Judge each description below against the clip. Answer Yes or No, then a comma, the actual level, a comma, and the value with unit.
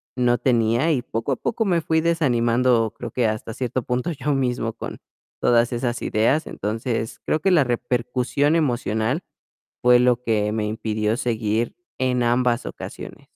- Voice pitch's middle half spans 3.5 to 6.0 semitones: No, narrow, 2.4 semitones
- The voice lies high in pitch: No, low, 120 Hz